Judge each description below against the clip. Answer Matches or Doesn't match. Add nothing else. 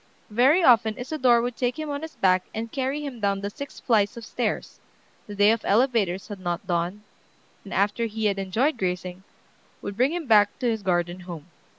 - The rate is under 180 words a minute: Doesn't match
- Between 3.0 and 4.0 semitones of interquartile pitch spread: Doesn't match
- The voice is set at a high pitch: Matches